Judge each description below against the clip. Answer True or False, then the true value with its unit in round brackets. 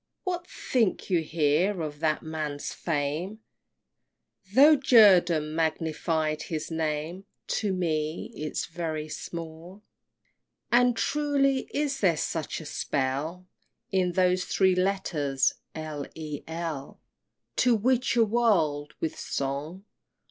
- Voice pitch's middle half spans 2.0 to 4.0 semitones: False (4.8 semitones)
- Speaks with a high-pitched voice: False (165 Hz)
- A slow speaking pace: True (115 wpm)